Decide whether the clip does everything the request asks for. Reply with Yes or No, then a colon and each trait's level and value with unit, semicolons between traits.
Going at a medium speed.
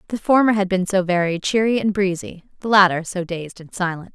No: fast, 215 wpm